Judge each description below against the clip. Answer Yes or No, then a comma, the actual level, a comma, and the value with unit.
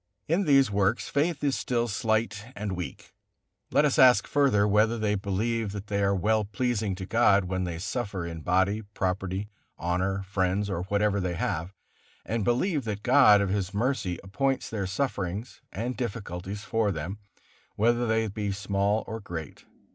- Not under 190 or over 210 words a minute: No, average, 165 wpm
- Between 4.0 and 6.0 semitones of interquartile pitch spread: No, average, 3.4 semitones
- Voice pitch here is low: Yes, low, 105 Hz